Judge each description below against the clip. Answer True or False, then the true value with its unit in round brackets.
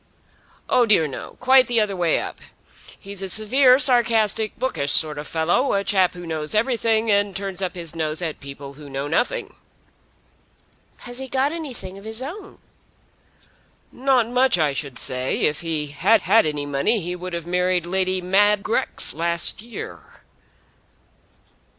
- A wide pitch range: True (6.1 semitones)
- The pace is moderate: True (160 wpm)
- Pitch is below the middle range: False (190 Hz)